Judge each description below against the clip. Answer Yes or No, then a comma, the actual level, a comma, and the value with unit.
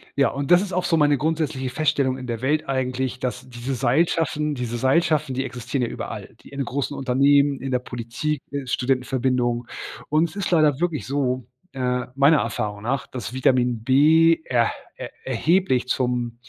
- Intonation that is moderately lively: Yes, average, 3.1 semitones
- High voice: No, low, 130 Hz